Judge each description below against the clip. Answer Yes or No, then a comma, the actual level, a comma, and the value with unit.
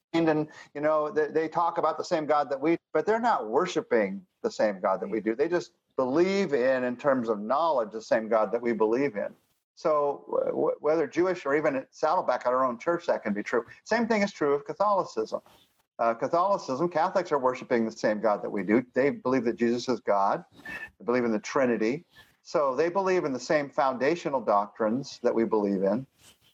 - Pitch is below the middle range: No, medium, 150 Hz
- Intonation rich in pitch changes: Yes, wide, 6.9 semitones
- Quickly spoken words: Yes, fast, 210 wpm